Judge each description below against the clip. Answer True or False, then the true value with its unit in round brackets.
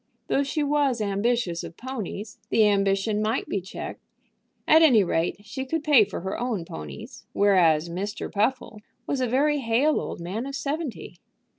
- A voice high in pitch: True (220 Hz)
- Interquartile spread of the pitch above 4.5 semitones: True (5.6 semitones)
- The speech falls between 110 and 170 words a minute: True (165 wpm)